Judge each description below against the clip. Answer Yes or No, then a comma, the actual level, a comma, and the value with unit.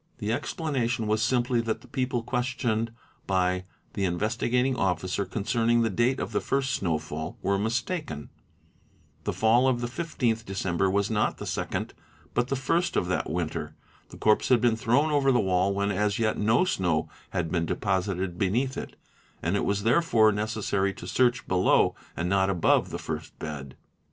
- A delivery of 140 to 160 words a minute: No, average, 175 wpm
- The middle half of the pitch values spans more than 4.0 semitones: Yes, average, 4.5 semitones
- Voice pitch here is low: Yes, low, 110 Hz